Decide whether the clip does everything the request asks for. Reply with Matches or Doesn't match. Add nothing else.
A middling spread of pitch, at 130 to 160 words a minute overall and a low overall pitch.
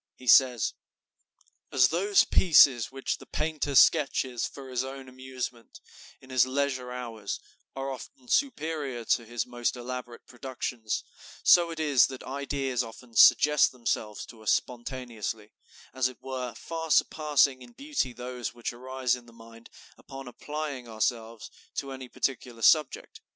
Doesn't match